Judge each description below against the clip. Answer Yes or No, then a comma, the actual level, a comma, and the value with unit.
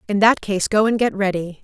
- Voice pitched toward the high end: Yes, high, 205 Hz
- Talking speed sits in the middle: No, fast, 260 wpm